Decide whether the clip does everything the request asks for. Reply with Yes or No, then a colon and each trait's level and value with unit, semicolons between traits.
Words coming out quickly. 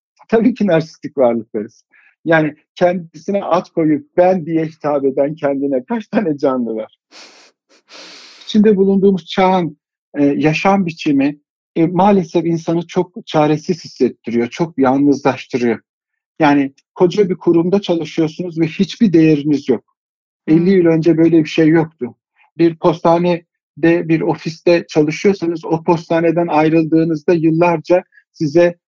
No: average, 120 wpm